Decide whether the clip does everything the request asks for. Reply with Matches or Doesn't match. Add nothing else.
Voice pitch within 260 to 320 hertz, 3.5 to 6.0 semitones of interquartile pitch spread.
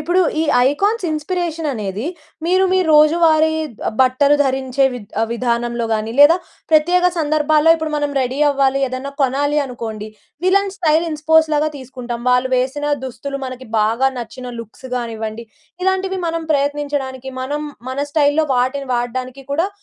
Matches